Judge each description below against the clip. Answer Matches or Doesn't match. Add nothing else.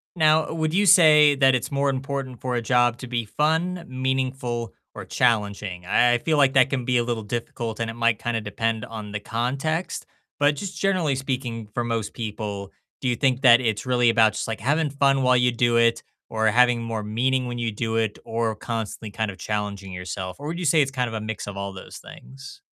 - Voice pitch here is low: Matches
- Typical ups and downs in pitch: Matches